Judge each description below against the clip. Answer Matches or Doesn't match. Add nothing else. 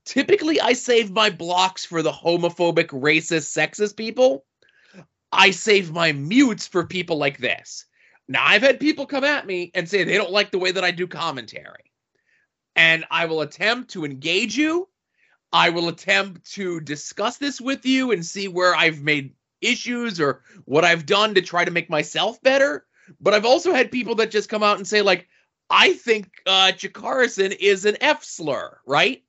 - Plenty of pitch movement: Matches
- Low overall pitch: Doesn't match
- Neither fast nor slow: Matches